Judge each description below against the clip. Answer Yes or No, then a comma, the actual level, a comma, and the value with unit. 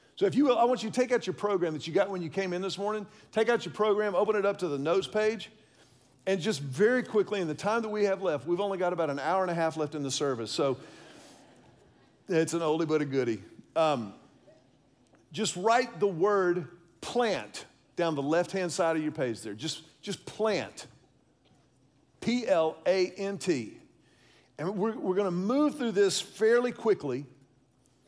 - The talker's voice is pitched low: No, high, 190 Hz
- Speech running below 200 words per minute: No, fast, 205 wpm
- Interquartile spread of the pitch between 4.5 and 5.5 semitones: Yes, average, 5.2 semitones